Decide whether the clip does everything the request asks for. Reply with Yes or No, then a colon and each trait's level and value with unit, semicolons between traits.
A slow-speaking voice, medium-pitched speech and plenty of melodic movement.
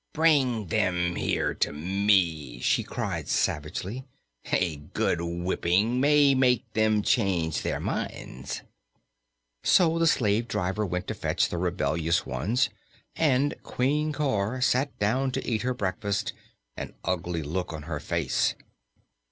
No: slow, 130 wpm; low, 100 Hz; wide, 6.9 semitones